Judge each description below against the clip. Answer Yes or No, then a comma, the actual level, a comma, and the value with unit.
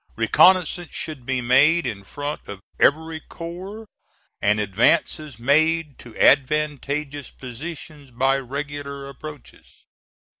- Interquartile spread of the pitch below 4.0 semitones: Yes, average, 3.6 semitones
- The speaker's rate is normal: No, slow, 105 wpm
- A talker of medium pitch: Yes, medium, 145 Hz